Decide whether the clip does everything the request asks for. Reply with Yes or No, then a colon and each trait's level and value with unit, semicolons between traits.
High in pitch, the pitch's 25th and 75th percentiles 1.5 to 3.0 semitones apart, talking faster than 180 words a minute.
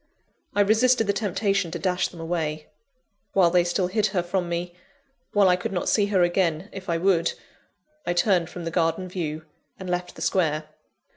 No: medium, 180 Hz; narrow, 2.5 semitones; average, 190 wpm